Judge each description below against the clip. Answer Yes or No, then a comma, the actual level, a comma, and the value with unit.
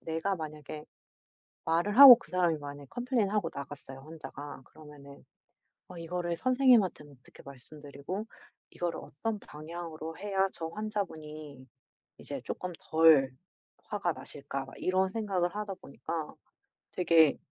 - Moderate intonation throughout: Yes, average, 4.6 semitones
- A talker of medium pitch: Yes, medium, 165 Hz